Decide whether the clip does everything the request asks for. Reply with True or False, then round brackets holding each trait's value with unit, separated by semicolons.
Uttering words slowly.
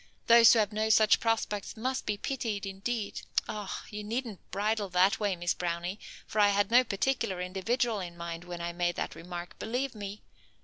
False (190 wpm)